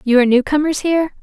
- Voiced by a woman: Yes, female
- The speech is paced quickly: Yes, fast, 245 wpm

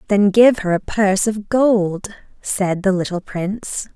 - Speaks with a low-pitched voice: No, high, 200 Hz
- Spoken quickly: No, average, 165 wpm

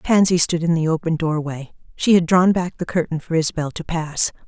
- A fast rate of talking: Yes, fast, 215 wpm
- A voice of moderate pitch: Yes, medium, 165 Hz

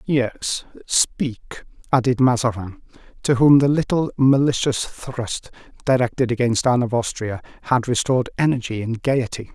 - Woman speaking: No, male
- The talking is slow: Yes, slow, 125 wpm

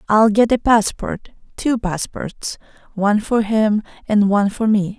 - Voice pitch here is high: Yes, high, 215 Hz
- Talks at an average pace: Yes, average, 155 wpm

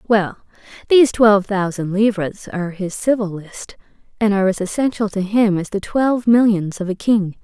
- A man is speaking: No, female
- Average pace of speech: Yes, average, 180 wpm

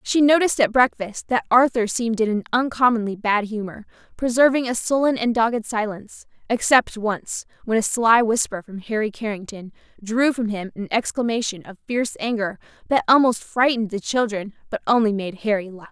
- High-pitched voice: Yes, high, 225 Hz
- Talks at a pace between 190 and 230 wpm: No, average, 170 wpm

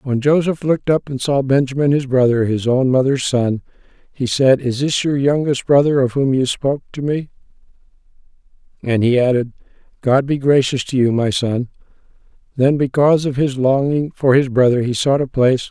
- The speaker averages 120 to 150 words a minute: No, average, 200 wpm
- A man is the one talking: Yes, male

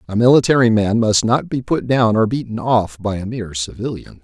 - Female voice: No, male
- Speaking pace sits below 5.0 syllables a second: No, 5.4 syllables/s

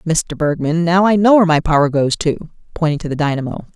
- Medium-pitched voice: Yes, medium, 160 Hz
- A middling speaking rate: No, fast, 225 wpm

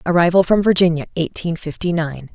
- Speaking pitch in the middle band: Yes, medium, 170 Hz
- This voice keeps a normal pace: Yes, average, 155 wpm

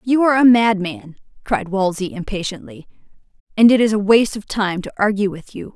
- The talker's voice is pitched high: Yes, high, 210 Hz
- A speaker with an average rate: Yes, average, 190 wpm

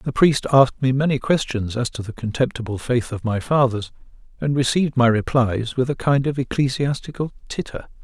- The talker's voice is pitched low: Yes, low, 125 Hz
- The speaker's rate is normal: Yes, average, 180 wpm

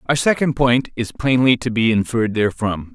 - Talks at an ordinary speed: Yes, average, 185 wpm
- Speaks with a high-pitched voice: No, low, 120 Hz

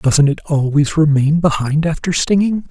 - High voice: No, medium, 155 Hz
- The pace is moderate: Yes, average, 155 wpm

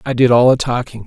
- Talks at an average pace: No, fast, 280 wpm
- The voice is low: Yes, low, 120 Hz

